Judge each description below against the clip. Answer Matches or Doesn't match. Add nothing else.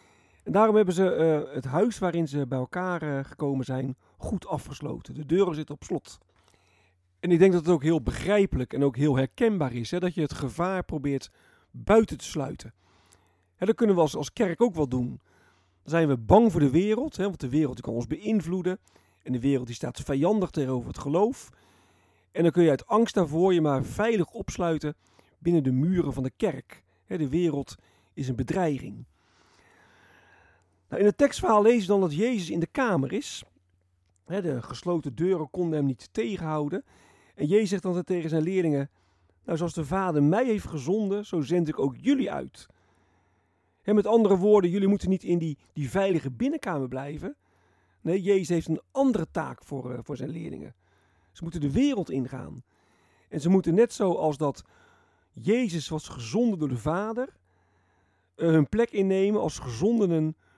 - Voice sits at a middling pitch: Matches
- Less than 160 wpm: Doesn't match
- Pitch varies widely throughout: Matches